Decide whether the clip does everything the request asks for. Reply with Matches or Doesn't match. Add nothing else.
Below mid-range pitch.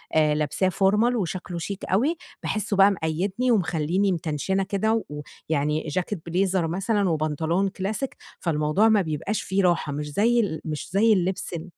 Doesn't match